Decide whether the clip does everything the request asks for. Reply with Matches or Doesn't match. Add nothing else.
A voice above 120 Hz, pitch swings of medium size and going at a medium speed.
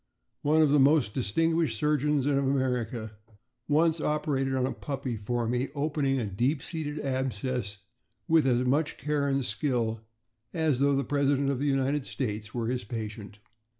Matches